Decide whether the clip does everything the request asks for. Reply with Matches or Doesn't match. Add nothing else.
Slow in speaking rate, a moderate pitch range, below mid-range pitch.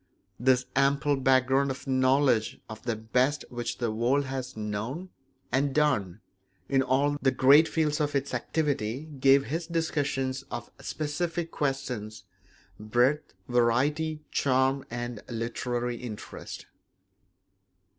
Matches